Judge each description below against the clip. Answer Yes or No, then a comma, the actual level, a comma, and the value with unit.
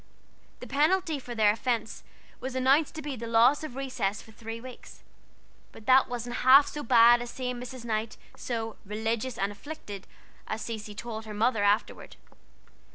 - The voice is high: Yes, high, 235 Hz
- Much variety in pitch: No, average, 3.0 semitones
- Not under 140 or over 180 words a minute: Yes, average, 165 wpm